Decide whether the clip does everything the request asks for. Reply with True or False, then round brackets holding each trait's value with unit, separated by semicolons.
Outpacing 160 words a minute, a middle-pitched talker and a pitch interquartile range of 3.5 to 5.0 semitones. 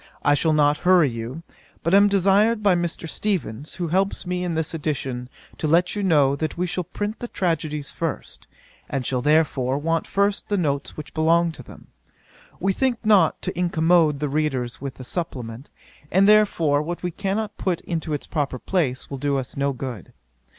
True (185 wpm; 160 Hz; 4.5 semitones)